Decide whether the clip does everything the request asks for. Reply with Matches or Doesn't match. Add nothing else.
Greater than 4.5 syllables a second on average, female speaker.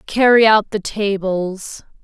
Doesn't match